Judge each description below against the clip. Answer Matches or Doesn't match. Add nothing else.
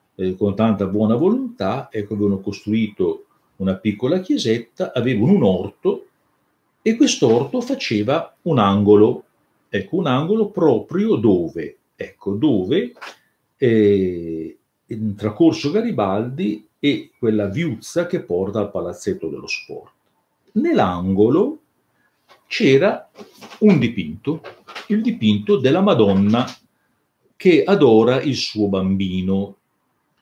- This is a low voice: Matches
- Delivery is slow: Matches